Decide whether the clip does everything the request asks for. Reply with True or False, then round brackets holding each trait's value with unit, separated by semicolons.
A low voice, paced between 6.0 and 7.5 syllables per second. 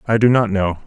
False (105 Hz; 5.4 syllables/s)